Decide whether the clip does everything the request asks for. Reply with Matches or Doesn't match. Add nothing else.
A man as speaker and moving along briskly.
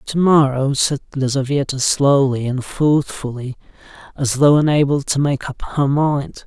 Doesn't match